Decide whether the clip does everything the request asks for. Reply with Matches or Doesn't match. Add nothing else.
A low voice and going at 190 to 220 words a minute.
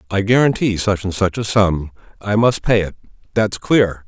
Doesn't match